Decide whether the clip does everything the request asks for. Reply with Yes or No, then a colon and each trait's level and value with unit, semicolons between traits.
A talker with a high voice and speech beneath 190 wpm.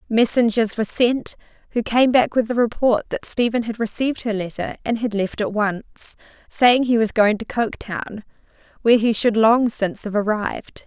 Yes: high, 225 Hz; average, 180 wpm